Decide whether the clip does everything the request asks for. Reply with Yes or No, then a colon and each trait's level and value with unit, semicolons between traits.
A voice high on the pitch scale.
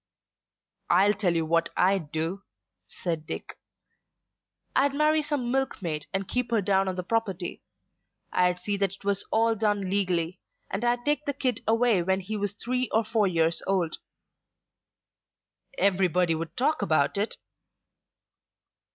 Yes: high, 195 Hz